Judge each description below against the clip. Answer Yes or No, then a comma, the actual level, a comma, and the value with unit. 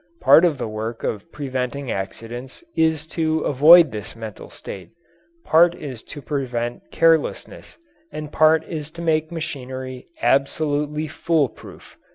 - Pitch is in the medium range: Yes, medium, 145 Hz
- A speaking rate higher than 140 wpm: No, slow, 135 wpm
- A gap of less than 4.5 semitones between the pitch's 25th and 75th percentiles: Yes, average, 4.1 semitones